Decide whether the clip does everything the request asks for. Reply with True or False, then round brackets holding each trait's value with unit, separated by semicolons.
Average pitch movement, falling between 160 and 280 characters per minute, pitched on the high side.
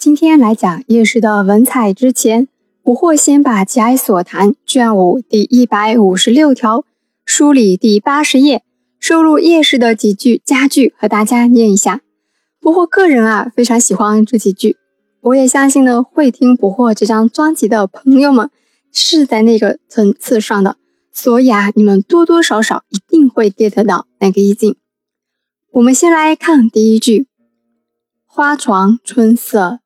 True (4.7 semitones; 235 characters per minute; 230 Hz)